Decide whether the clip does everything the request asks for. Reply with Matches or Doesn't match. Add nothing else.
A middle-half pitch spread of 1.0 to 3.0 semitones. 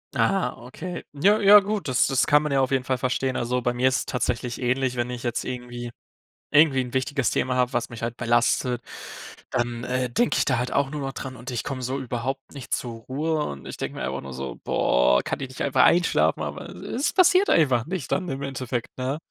Matches